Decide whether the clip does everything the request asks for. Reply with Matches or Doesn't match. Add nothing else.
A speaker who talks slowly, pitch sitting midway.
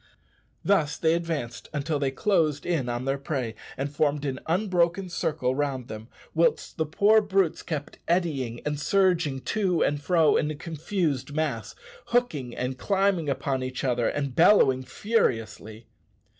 Doesn't match